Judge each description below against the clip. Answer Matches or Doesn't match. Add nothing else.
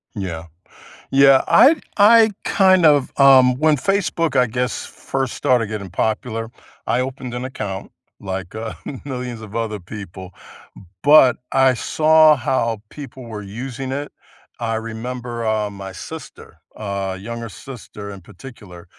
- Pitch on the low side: Matches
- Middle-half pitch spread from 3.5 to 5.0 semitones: Matches